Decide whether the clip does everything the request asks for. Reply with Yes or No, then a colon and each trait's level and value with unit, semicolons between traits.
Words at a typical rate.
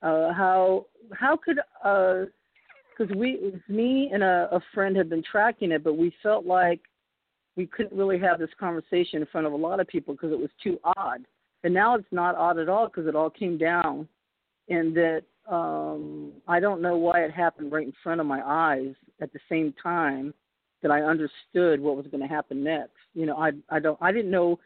No: fast, 215 wpm